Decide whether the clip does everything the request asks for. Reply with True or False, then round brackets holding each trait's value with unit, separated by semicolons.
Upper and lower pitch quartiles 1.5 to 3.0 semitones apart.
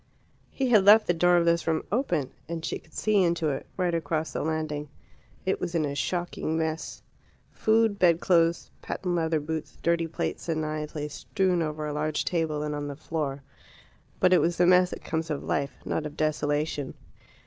True (2.5 semitones)